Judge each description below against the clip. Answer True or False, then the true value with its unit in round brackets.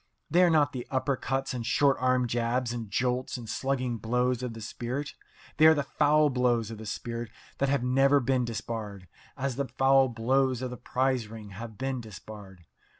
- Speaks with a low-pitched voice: True (125 Hz)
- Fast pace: False (195 wpm)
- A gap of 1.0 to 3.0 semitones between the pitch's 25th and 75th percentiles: True (2.7 semitones)